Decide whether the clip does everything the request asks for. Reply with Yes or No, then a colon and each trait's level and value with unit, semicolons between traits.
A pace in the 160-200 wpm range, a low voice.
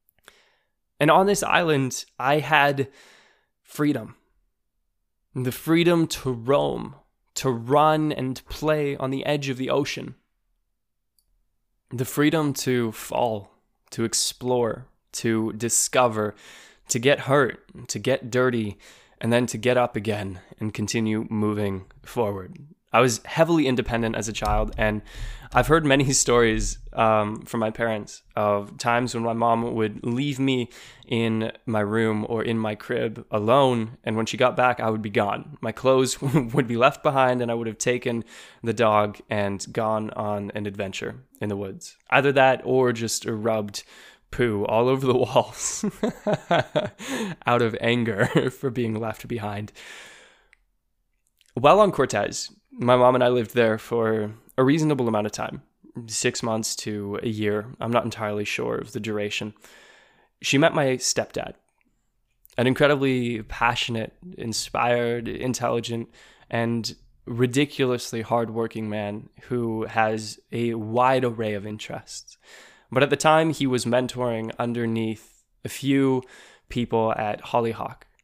No: average, 140 wpm; low, 120 Hz